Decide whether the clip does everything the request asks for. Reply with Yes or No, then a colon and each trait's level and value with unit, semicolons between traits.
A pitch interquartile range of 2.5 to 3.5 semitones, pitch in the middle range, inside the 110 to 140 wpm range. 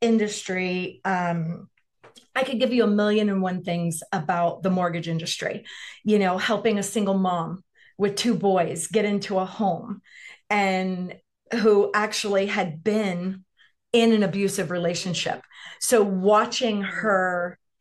No: average, 2.8 semitones; high, 195 Hz; slow, 135 wpm